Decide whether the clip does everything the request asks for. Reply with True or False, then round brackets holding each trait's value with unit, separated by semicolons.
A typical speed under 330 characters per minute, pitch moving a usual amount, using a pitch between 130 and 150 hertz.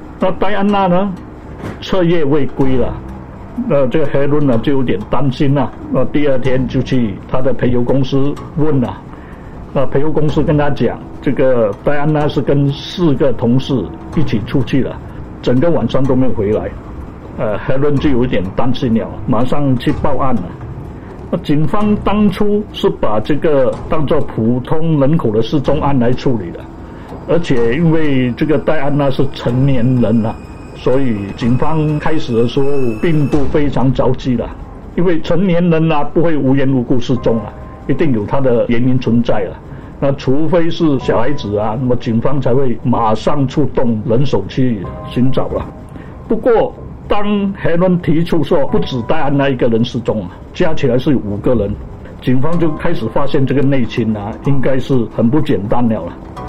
True (245 characters per minute; 4.1 semitones; 135 Hz)